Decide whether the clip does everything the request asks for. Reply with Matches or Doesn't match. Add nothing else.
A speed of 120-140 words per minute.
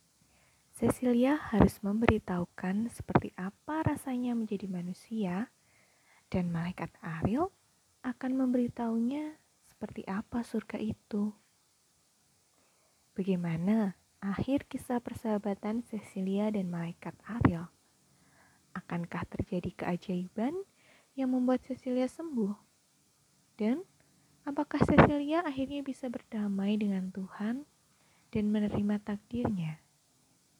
Doesn't match